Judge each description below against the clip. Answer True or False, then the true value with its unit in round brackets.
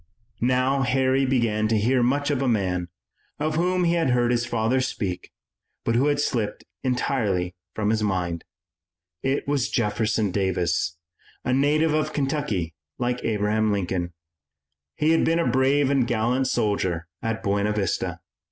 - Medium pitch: False (120 Hz)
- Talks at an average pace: True (150 wpm)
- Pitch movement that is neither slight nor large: True (4.6 semitones)